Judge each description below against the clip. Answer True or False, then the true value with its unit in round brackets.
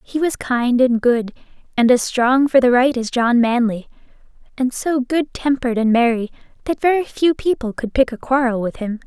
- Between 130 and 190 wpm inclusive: False (200 wpm)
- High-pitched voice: True (250 Hz)